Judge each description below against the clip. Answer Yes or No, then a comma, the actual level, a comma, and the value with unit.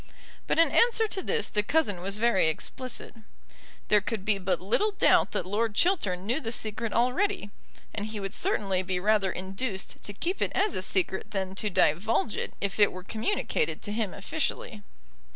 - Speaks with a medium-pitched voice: No, high, 210 Hz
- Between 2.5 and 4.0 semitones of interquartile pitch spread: No, average, 4.9 semitones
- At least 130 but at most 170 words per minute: No, average, 185 wpm